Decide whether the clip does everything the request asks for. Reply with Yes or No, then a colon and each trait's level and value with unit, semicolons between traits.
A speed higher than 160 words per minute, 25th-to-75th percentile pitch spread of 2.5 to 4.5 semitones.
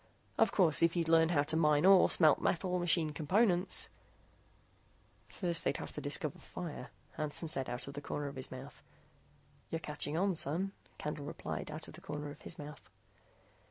Yes: average, 185 wpm; average, 3.0 semitones